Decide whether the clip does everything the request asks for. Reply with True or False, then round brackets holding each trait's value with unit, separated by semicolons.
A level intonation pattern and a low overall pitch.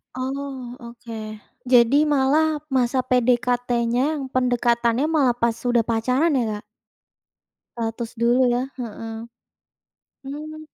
False (2.3 semitones; 245 Hz)